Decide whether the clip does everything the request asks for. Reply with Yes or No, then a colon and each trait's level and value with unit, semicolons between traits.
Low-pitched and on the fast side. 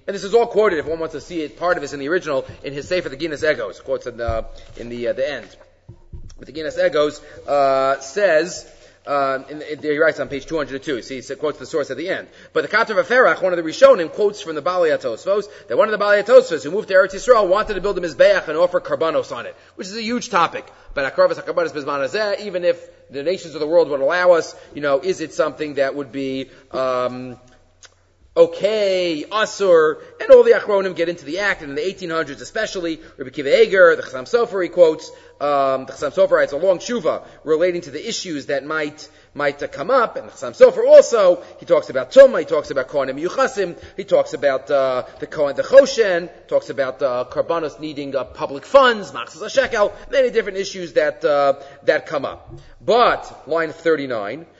No: medium, 180 Hz; fast, 220 wpm